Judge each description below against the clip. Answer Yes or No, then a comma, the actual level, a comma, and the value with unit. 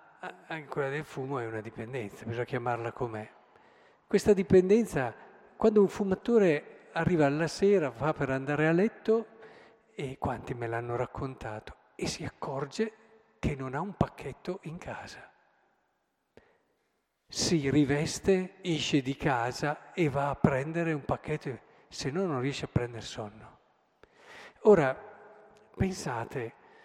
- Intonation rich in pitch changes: Yes, wide, 6.6 semitones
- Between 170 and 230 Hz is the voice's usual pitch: No, medium, 150 Hz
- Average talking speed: Yes, average, 125 wpm